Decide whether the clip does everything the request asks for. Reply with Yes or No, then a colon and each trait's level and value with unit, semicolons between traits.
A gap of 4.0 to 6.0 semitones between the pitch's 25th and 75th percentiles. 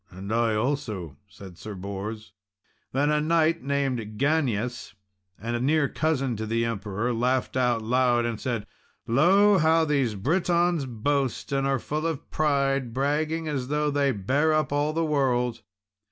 Yes: average, 4.7 semitones